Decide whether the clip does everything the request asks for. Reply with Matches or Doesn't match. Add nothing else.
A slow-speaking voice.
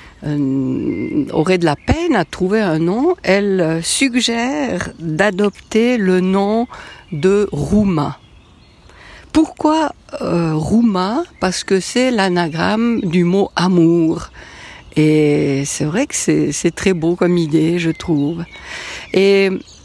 Matches